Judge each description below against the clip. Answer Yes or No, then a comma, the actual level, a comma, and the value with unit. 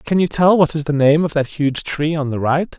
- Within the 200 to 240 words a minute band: No, fast, 300 wpm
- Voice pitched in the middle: Yes, medium, 155 Hz